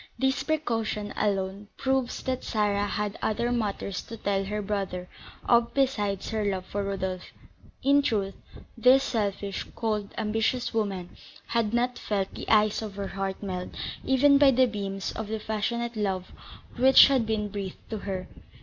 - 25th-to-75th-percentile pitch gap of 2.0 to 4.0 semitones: Yes, average, 3.2 semitones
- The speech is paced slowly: No, average, 160 wpm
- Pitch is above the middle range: Yes, high, 210 Hz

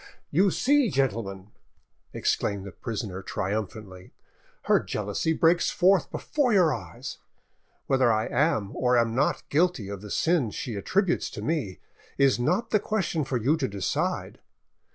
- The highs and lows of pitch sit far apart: Yes, wide, 8.9 semitones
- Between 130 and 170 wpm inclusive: Yes, average, 145 wpm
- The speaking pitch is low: Yes, low, 130 Hz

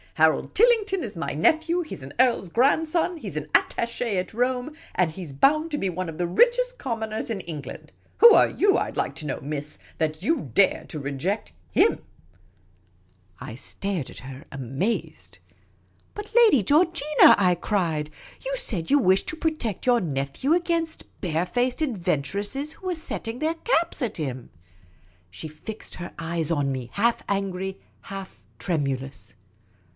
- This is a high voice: Yes, high, 200 Hz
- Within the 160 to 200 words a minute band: Yes, average, 175 wpm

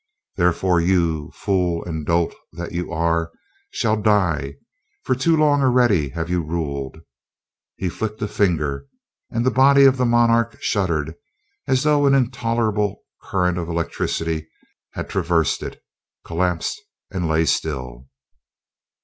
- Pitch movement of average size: No, wide, 6.1 semitones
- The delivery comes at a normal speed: No, slow, 130 wpm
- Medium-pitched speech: No, very low, 90 Hz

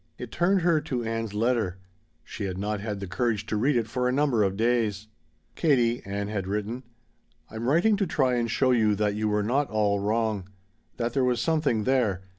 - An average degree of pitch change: Yes, average, 3.4 semitones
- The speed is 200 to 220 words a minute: Yes, fast, 205 wpm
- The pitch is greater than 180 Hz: No, low, 115 Hz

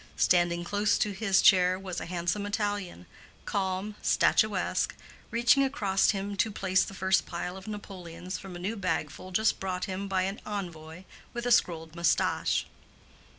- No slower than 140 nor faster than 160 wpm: Yes, average, 155 wpm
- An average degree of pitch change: No, narrow, 2.3 semitones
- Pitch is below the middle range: No, high, 190 Hz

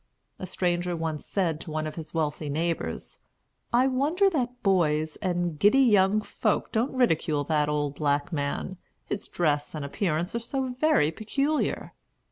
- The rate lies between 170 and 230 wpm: No, average, 155 wpm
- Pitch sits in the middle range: Yes, medium, 175 Hz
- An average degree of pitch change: No, wide, 7.3 semitones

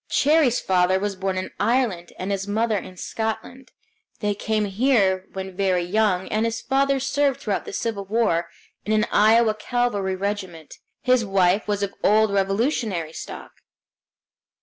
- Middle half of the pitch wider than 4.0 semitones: No, average, 3.3 semitones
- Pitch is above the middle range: Yes, high, 205 Hz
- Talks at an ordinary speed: Yes, average, 150 wpm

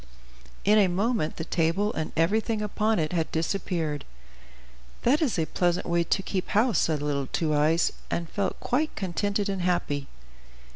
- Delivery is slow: No, average, 160 wpm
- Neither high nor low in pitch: Yes, medium, 180 Hz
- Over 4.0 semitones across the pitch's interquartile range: Yes, average, 4.4 semitones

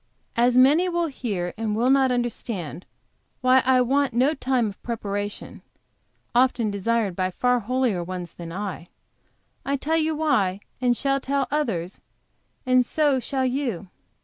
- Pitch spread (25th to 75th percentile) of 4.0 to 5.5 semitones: Yes, average, 4.9 semitones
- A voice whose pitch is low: No, high, 245 Hz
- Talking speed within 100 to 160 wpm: Yes, average, 145 wpm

